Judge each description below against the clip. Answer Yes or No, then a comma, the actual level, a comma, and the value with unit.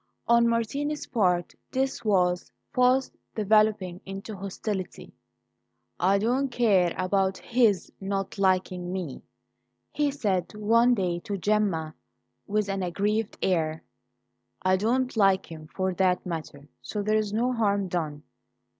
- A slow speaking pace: Yes, slow, 125 wpm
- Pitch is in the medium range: No, high, 200 Hz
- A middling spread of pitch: Yes, average, 3.6 semitones